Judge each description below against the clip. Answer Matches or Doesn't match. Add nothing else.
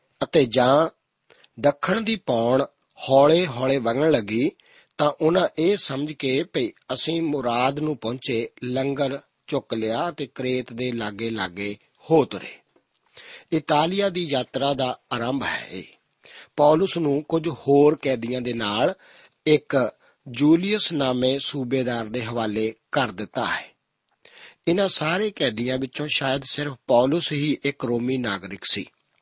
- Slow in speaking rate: Doesn't match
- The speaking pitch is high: Doesn't match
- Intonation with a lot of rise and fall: Doesn't match